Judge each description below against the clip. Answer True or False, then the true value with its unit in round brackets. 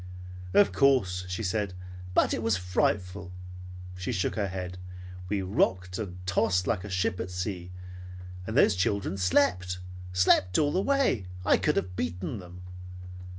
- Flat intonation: True (2.1 semitones)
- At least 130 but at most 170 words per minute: True (150 wpm)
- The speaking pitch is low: True (95 Hz)